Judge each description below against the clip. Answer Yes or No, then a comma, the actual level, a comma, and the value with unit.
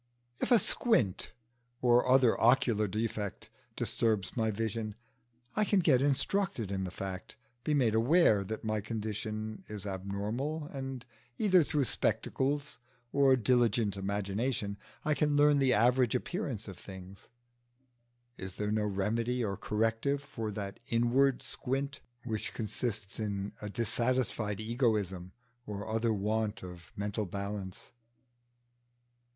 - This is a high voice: No, low, 110 Hz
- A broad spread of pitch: No, average, 4.3 semitones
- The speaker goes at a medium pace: No, slow, 125 wpm